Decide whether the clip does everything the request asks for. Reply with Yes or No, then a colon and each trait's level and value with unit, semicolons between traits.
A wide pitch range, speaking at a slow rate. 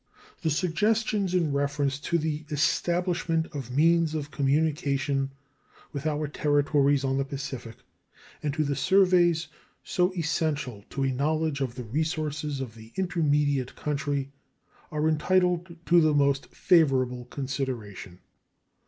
No: average, 3.1 semitones; slow, 125 wpm